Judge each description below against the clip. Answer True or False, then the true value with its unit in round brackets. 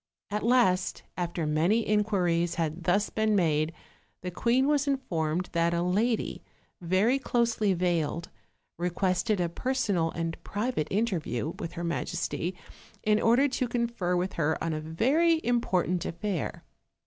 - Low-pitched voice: False (185 Hz)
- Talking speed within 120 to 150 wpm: True (140 wpm)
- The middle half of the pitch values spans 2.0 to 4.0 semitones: False (5.4 semitones)